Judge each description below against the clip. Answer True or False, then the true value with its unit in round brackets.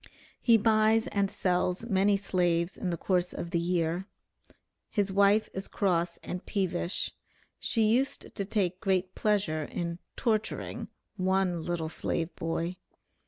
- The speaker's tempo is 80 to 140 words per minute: True (135 wpm)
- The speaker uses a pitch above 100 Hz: True (185 Hz)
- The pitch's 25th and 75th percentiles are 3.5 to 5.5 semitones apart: False (2.8 semitones)